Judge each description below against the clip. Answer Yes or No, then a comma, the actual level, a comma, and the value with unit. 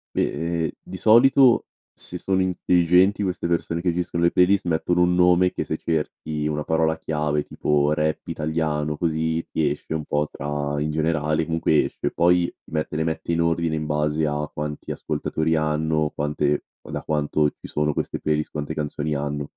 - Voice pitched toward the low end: Yes, very low, 80 Hz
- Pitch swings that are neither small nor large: No, narrow, 2.1 semitones